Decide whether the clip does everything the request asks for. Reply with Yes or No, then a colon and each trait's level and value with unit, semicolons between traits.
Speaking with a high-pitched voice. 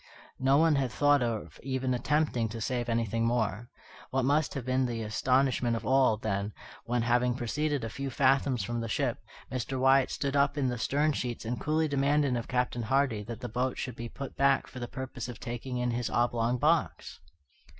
No: low, 125 Hz